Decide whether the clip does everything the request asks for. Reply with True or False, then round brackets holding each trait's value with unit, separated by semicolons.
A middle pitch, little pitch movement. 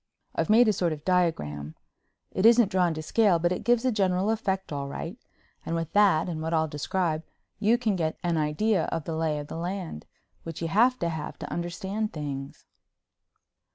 False (175 Hz; 4.5 semitones)